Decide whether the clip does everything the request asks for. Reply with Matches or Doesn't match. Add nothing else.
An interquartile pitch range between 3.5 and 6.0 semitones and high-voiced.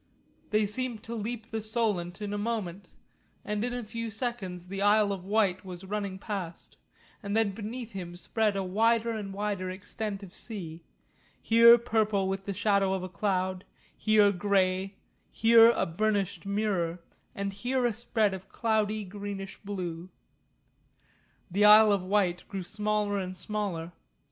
Doesn't match